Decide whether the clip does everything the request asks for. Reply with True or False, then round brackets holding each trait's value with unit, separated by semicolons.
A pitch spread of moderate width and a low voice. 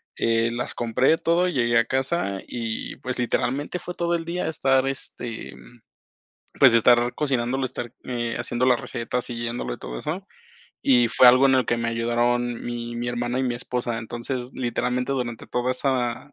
False (1.9 semitones; 120 Hz)